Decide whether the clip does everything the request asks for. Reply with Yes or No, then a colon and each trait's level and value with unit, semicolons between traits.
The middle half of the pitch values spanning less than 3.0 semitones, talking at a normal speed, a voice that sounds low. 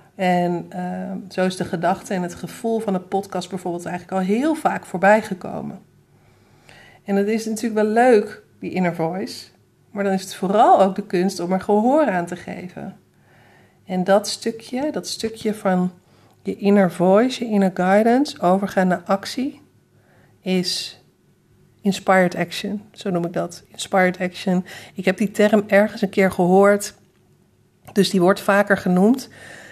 No: narrow, 2.5 semitones; average, 160 wpm; high, 195 Hz